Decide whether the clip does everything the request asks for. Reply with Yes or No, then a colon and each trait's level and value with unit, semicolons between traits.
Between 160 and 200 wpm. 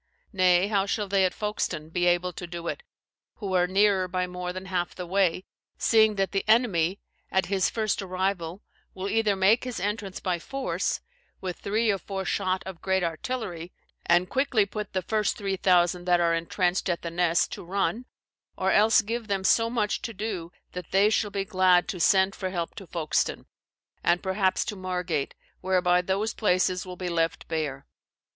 Yes: average, 185 wpm